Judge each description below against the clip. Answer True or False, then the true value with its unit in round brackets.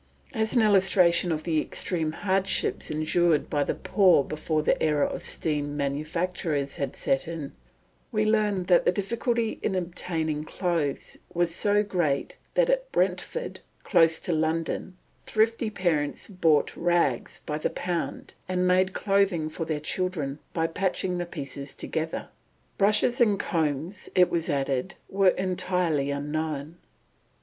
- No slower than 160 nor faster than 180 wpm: False (140 wpm)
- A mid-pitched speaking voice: True (170 Hz)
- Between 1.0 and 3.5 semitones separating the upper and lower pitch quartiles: False (3.9 semitones)